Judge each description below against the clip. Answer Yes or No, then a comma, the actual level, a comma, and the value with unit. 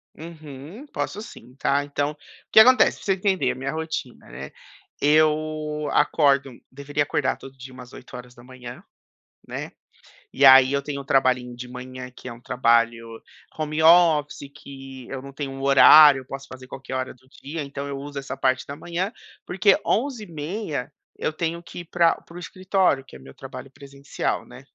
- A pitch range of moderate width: Yes, average, 3.2 semitones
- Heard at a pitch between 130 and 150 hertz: Yes, medium, 140 Hz